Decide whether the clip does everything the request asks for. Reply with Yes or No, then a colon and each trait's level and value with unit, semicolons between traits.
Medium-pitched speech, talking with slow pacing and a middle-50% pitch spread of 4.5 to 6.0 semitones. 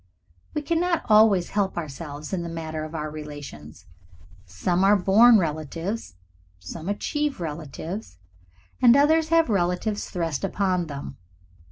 Yes: medium, 175 Hz; slow, 130 wpm; wide, 5.6 semitones